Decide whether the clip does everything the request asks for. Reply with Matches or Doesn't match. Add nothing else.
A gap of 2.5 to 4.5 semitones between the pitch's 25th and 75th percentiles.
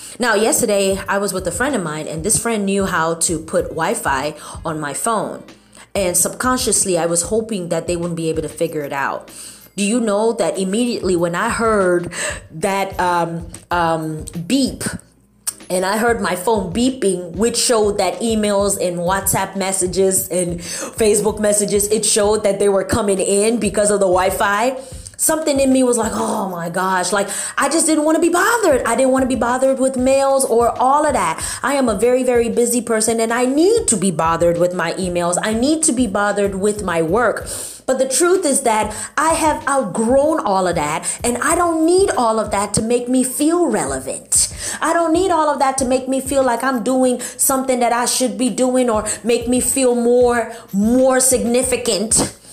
Doesn't match